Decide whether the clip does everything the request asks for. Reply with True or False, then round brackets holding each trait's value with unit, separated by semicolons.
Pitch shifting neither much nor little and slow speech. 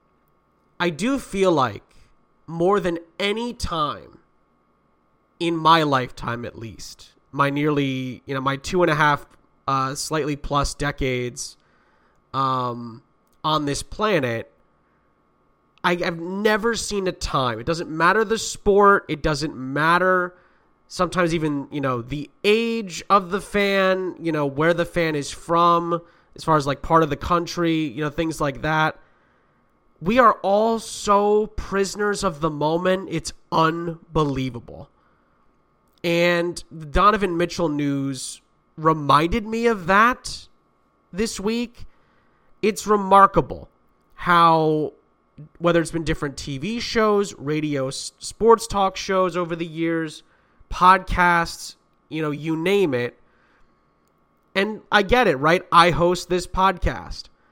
True (4.6 semitones; 130 wpm)